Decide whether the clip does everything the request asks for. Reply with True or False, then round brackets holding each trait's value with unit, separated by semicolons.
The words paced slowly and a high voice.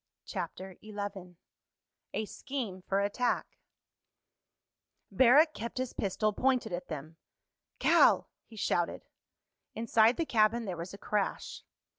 True (115 wpm; 210 Hz)